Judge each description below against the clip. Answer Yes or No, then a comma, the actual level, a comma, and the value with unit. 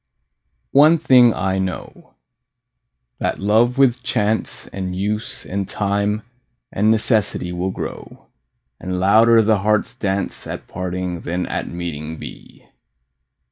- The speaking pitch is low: Yes, low, 100 Hz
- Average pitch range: Yes, average, 3.4 semitones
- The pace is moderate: No, slow, 120 wpm